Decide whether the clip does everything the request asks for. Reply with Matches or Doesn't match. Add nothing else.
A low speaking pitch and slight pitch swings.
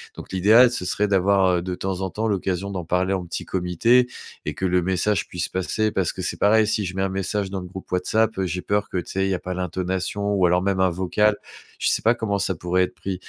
Matches